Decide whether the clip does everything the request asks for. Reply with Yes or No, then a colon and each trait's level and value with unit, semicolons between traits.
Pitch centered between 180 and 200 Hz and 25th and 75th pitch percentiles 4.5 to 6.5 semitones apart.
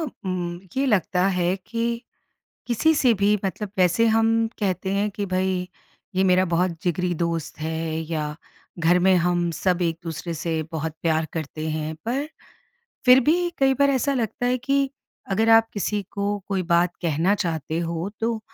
Yes: medium, 185 Hz; average, 5.0 semitones